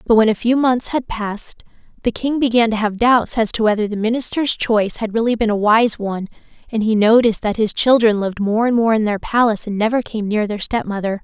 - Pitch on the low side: No, high, 220 Hz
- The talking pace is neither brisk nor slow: No, fast, 235 wpm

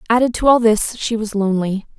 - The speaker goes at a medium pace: No, fast, 210 wpm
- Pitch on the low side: No, high, 220 Hz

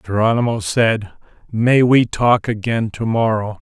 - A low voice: Yes, low, 110 Hz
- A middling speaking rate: No, slow, 115 wpm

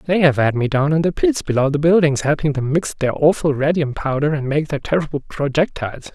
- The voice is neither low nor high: Yes, medium, 145 Hz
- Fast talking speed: Yes, fast, 225 wpm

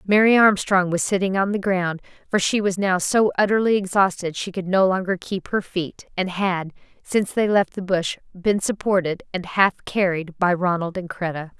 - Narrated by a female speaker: Yes, female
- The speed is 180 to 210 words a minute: Yes, average, 190 wpm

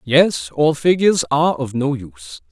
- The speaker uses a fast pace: No, average, 165 wpm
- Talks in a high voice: No, medium, 140 Hz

